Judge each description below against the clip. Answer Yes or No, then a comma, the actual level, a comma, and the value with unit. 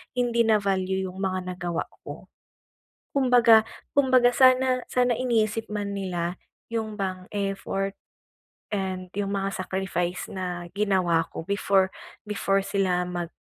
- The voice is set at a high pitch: Yes, high, 195 Hz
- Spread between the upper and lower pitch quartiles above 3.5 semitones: No, average, 3.2 semitones